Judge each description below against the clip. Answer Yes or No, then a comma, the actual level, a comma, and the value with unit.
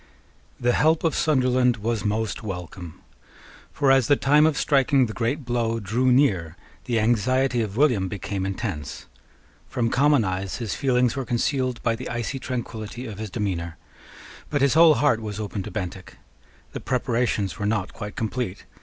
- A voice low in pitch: Yes, low, 115 Hz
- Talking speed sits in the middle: Yes, average, 165 wpm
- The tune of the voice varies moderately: Yes, average, 4.0 semitones